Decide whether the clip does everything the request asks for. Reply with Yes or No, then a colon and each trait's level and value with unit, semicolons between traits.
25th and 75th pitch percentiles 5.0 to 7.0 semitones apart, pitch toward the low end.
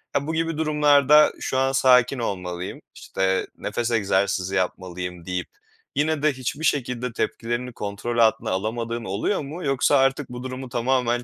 Yes: wide, 5.5 semitones; low, 125 Hz